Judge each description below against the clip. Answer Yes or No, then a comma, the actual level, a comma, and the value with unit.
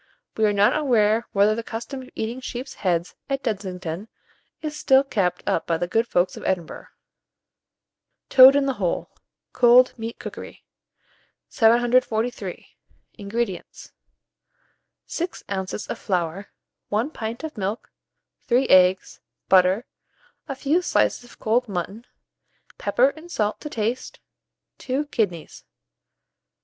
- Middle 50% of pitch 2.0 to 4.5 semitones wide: No, average, 4.9 semitones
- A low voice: No, high, 225 Hz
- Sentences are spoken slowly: Yes, slow, 125 wpm